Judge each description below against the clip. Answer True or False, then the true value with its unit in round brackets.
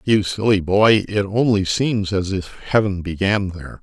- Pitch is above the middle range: False (100 Hz)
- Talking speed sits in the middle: True (170 wpm)